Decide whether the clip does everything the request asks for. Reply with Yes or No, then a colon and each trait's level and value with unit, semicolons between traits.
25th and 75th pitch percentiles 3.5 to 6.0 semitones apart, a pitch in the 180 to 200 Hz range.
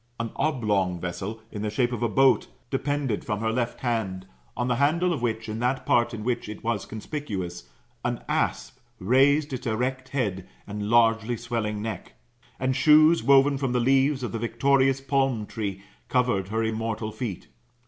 No: average, 3.9 semitones; low, 120 Hz